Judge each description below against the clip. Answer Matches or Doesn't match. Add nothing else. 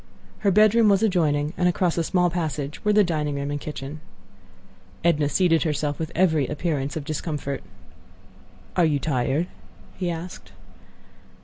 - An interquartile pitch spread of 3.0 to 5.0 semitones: Matches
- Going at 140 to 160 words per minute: Matches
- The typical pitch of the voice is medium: Matches